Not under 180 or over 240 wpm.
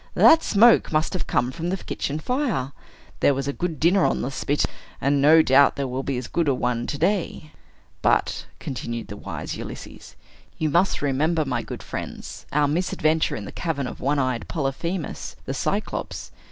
Yes: average, 185 wpm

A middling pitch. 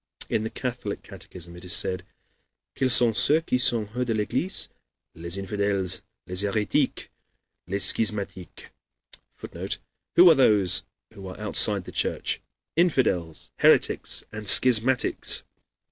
No: low, 105 Hz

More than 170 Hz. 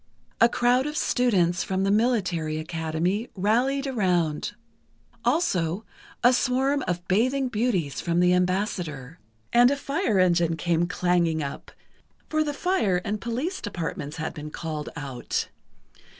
Yes: medium, 185 Hz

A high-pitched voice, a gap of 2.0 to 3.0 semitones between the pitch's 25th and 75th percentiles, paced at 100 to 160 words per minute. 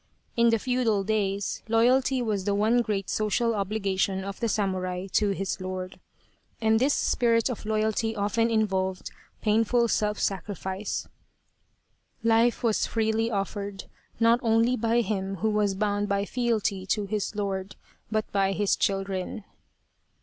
Yes: high, 210 Hz; narrow, 2.6 semitones; average, 140 wpm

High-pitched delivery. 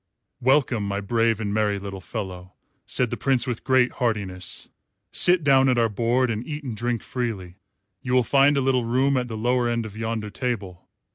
No: low, 115 Hz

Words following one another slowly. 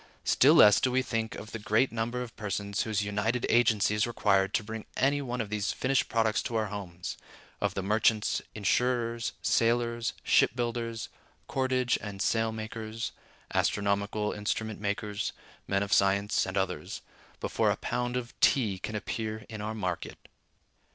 No: average, 160 wpm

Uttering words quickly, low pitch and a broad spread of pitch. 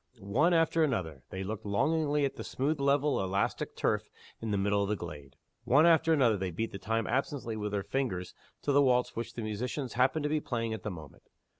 Yes: fast, 215 wpm; low, 115 Hz; wide, 6.0 semitones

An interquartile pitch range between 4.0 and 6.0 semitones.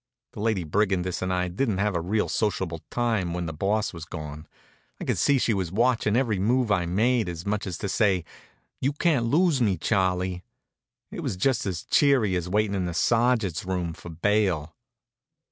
Yes: average, 4.3 semitones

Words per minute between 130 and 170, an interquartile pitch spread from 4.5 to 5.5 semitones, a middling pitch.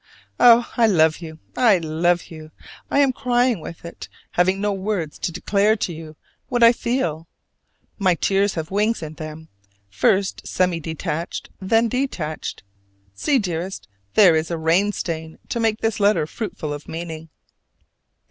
Yes: average, 155 wpm; average, 5.1 semitones; medium, 180 Hz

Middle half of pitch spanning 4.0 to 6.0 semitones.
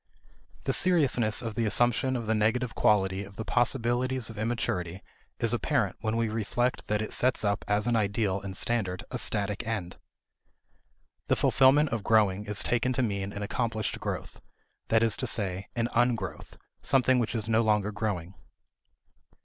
No: average, 3.0 semitones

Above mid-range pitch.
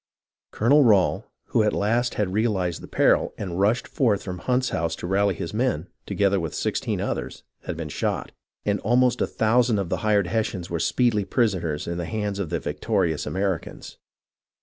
No: low, 100 Hz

